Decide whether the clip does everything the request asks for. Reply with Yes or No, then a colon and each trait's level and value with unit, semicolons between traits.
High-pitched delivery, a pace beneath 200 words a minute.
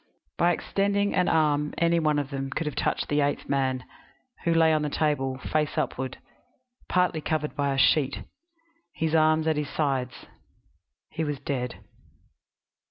No: medium, 150 Hz; average, 160 wpm